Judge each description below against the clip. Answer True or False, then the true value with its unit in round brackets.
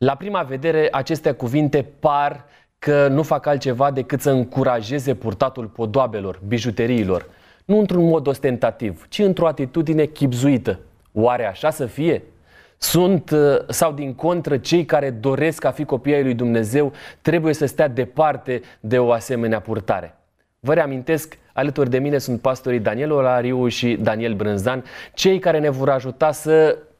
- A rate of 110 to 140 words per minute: False (150 wpm)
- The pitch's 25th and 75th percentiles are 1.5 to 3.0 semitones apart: False (4.0 semitones)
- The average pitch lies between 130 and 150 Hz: True (135 Hz)